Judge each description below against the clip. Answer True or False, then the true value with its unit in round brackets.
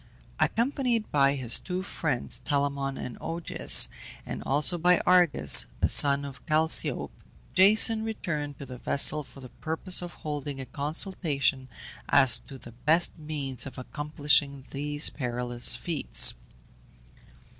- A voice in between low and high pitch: True (145 Hz)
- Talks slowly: True (130 wpm)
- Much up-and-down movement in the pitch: False (3.9 semitones)